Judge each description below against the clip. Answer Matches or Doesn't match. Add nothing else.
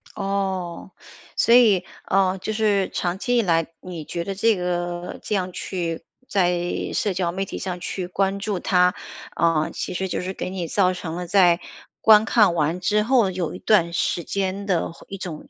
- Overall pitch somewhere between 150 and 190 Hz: Matches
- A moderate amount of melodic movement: Doesn't match